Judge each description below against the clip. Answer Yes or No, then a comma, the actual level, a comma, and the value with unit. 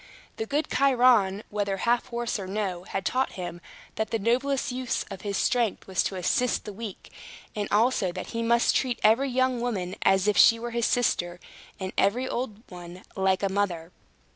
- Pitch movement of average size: Yes, average, 4.2 semitones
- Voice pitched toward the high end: Yes, high, 215 Hz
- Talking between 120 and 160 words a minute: No, average, 190 wpm